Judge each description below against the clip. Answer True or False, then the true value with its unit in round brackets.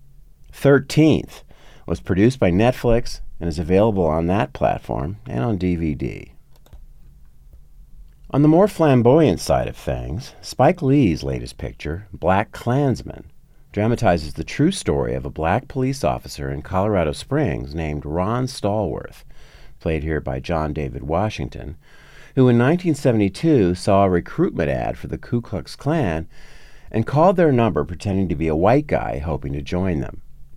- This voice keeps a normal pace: True (145 wpm)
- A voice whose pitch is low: True (95 Hz)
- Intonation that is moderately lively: False (8.3 semitones)